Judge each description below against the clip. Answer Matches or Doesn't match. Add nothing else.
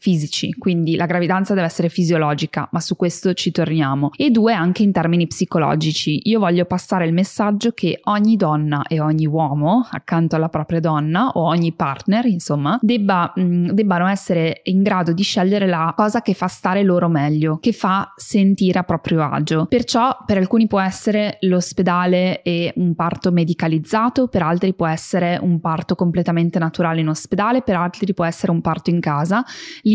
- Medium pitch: Matches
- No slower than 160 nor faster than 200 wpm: Matches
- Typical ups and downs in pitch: Matches